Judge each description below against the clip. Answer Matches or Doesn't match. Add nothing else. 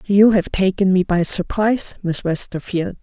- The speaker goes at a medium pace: Matches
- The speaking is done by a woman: Matches